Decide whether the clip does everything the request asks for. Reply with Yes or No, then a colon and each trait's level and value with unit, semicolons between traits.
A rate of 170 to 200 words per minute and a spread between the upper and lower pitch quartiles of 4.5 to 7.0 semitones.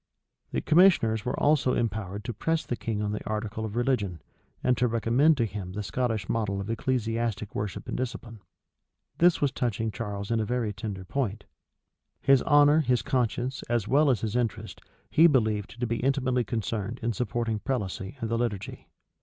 No: average, 180 wpm; average, 3.3 semitones